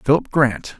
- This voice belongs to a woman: No, male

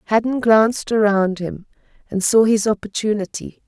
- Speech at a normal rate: No, slow, 130 wpm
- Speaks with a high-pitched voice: Yes, high, 210 Hz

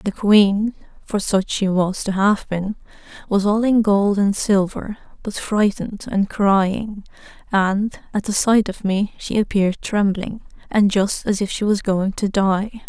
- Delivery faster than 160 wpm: Yes, average, 170 wpm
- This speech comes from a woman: Yes, female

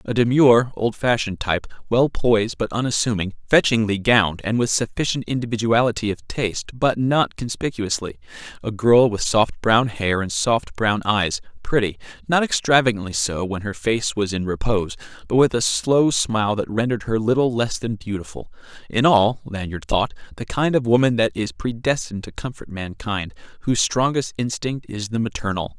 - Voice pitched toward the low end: Yes, low, 110 Hz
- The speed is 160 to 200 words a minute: Yes, average, 165 wpm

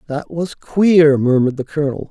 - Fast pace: No, average, 170 wpm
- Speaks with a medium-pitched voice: Yes, medium, 150 Hz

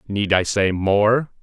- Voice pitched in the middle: No, low, 105 Hz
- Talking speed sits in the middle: Yes, average, 170 wpm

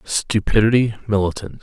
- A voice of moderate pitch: No, low, 105 Hz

